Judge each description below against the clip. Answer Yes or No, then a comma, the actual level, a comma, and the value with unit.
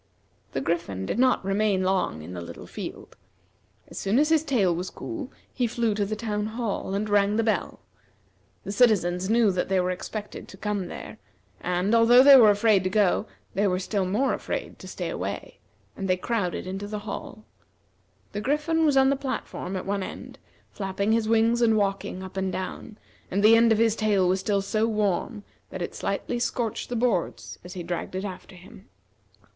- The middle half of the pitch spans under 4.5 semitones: Yes, average, 3.4 semitones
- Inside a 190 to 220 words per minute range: Yes, average, 195 wpm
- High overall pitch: Yes, high, 205 Hz